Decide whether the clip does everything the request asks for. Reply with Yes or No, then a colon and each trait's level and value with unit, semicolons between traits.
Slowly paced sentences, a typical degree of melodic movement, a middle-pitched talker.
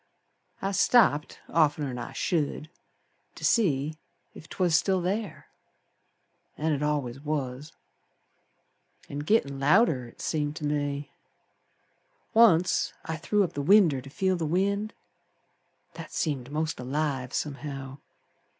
Yes: slow, 120 wpm; average, 4.4 semitones; medium, 150 Hz